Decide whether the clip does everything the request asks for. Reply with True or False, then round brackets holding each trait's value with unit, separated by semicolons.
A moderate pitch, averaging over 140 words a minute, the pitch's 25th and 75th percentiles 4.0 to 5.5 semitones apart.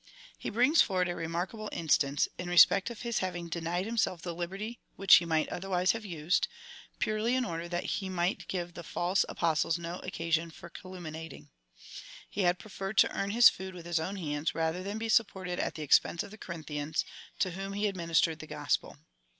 False (175 Hz; 200 wpm; 3.0 semitones)